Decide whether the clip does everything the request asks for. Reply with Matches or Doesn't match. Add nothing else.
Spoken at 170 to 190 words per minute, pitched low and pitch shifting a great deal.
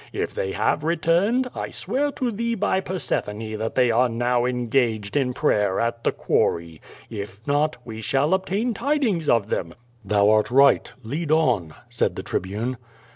Matches